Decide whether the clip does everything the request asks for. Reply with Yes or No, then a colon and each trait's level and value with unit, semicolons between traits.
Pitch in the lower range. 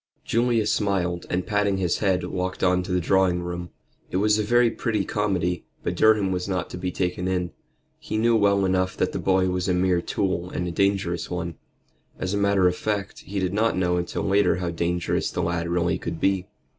Yes: very low, 95 Hz